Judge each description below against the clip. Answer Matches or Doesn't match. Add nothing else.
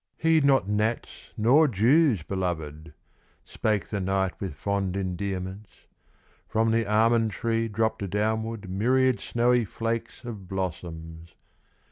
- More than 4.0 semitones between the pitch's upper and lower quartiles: Doesn't match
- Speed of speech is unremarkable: Doesn't match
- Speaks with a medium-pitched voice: Doesn't match